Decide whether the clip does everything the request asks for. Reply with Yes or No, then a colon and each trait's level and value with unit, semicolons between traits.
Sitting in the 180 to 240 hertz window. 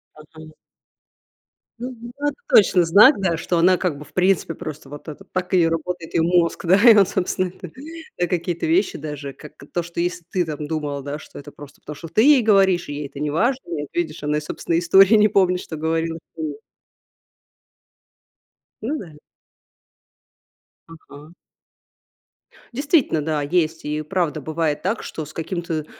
No: medium, 165 Hz